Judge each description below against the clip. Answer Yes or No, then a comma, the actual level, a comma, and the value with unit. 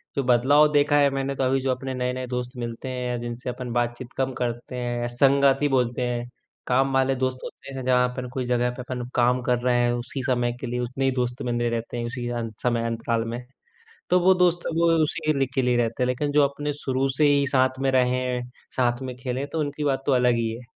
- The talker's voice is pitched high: No, low, 125 Hz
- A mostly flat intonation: Yes, narrow, 1.8 semitones